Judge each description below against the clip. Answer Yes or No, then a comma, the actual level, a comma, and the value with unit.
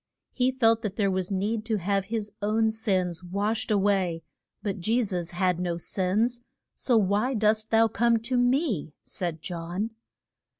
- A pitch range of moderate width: Yes, average, 3.5 semitones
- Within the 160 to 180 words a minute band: Yes, average, 165 wpm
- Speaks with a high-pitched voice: Yes, high, 205 Hz